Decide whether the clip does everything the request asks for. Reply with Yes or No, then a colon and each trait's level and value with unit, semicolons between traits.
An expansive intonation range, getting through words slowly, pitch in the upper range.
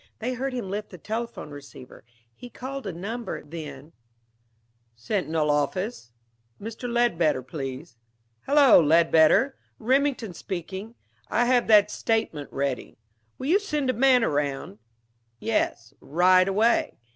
Yes: wide, 7.9 semitones; slow, 120 wpm; high, 200 Hz